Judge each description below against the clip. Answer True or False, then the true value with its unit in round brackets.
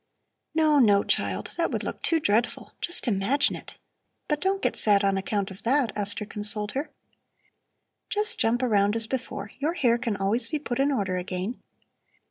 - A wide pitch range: True (5.7 semitones)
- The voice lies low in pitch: False (230 Hz)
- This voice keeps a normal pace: True (175 wpm)